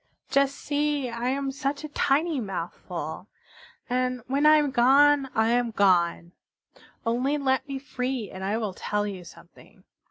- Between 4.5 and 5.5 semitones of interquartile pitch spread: Yes, average, 5.0 semitones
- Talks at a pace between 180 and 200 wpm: No, average, 155 wpm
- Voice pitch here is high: Yes, very high, 255 Hz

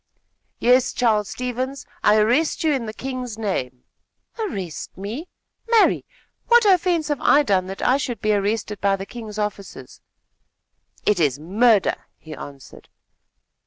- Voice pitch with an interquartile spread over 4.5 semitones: Yes, average, 5.1 semitones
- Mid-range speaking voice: No, high, 220 Hz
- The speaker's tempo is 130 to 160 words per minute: Yes, average, 140 wpm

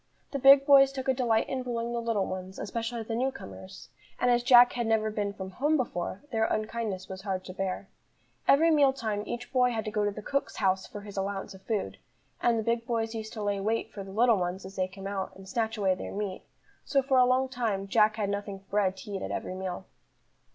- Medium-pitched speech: No, high, 215 Hz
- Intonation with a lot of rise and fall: No, average, 3.8 semitones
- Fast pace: Yes, fast, 240 wpm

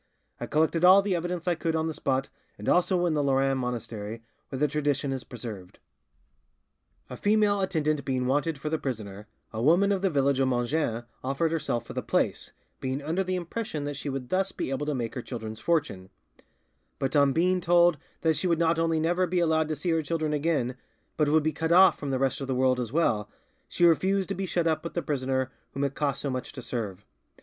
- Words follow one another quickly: Yes, fast, 225 wpm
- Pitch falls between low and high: Yes, medium, 150 Hz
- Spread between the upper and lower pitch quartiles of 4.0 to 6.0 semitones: Yes, average, 4.5 semitones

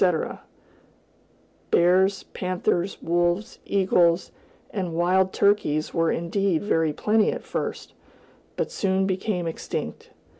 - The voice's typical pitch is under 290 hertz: Yes, medium, 185 Hz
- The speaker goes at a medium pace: No, slow, 105 wpm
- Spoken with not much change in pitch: Yes, narrow, 2.2 semitones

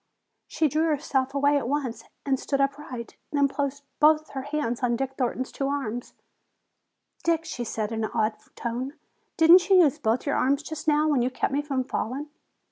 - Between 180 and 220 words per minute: Yes, average, 190 wpm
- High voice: Yes, very high, 275 Hz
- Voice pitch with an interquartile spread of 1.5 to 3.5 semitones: Yes, average, 2.9 semitones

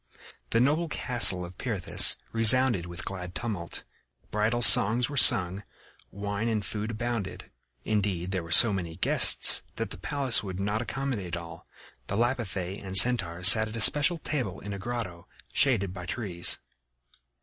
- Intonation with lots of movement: No, average, 4.6 semitones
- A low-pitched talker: Yes, low, 105 Hz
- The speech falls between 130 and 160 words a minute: Yes, average, 155 wpm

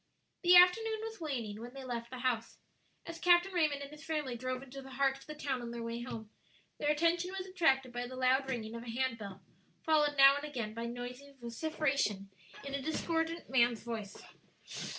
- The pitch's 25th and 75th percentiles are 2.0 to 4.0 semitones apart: No, average, 4.5 semitones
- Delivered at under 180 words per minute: No, average, 200 wpm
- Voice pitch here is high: Yes, very high, 265 Hz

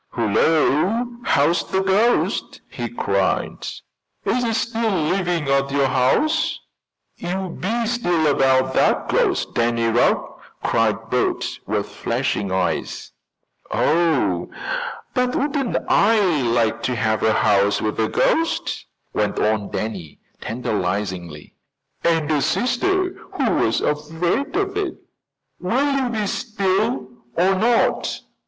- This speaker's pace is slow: Yes, slow, 120 wpm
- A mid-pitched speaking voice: Yes, medium, 160 Hz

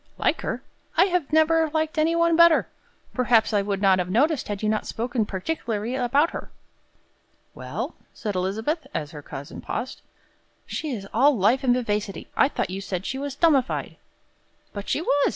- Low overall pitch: No, high, 245 Hz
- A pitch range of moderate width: No, wide, 7.3 semitones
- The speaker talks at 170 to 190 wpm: Yes, average, 175 wpm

